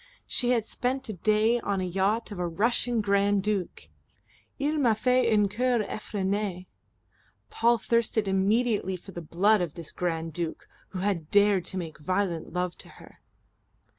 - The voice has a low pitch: No, high, 205 Hz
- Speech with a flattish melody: No, average, 3.9 semitones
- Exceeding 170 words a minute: No, average, 165 wpm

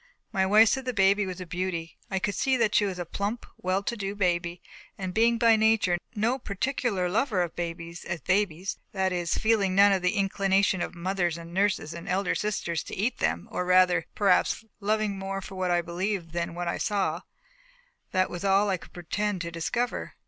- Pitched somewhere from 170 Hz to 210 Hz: Yes, high, 190 Hz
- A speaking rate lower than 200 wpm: No, fast, 205 wpm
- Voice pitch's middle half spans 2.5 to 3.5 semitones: Yes, average, 2.8 semitones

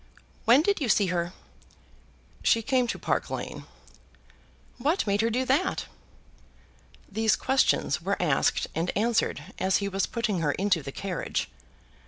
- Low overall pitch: No, high, 210 Hz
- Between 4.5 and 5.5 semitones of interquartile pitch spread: Yes, average, 5.0 semitones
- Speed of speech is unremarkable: Yes, average, 145 wpm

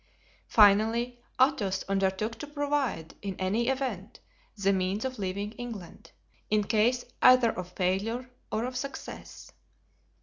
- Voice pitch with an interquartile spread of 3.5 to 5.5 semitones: Yes, average, 4.3 semitones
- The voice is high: Yes, high, 215 Hz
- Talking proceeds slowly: Yes, slow, 115 wpm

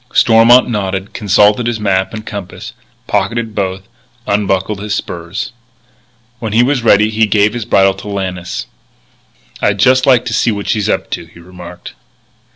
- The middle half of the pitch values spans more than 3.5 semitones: No, average, 2.8 semitones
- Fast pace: No, average, 160 wpm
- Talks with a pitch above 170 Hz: No, low, 105 Hz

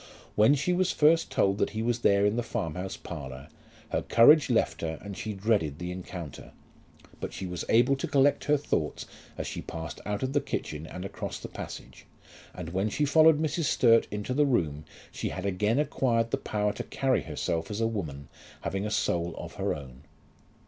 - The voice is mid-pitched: No, low, 105 Hz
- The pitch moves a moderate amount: No, wide, 7.1 semitones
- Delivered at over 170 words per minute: Yes, average, 200 wpm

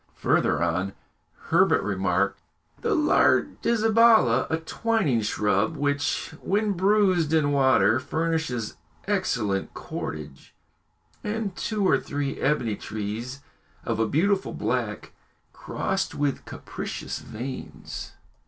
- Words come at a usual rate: No, slow, 100 wpm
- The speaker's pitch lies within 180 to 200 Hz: No, medium, 145 Hz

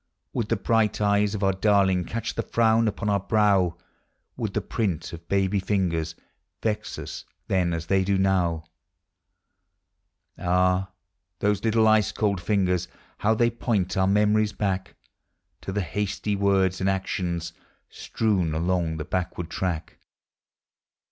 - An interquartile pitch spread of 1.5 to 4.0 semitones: Yes, narrow, 2.5 semitones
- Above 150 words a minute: No, average, 140 wpm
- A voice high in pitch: No, very low, 95 Hz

